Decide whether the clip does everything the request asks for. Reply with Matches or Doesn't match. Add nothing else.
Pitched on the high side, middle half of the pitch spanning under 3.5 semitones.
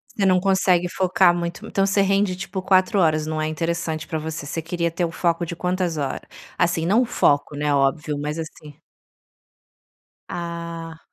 Doesn't match